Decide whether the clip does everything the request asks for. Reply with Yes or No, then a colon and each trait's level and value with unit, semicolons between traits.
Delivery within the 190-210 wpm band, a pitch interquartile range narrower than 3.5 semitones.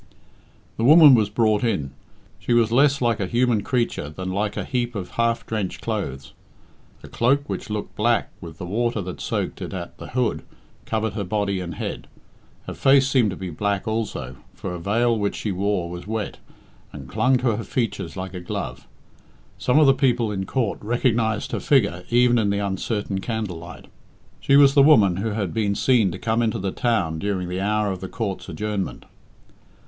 No: average, 195 wpm; average, 3.9 semitones